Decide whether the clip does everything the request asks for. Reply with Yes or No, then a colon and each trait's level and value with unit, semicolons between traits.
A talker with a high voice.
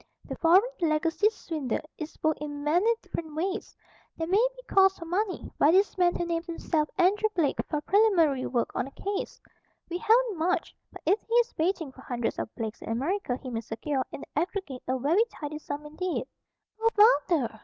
Yes: very high, 330 Hz